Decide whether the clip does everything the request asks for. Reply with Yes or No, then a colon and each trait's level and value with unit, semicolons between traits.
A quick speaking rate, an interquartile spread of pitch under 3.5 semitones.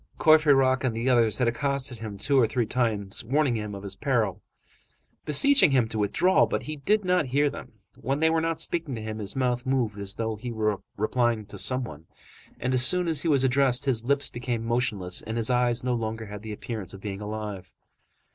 No: fast, 215 wpm; average, 4.1 semitones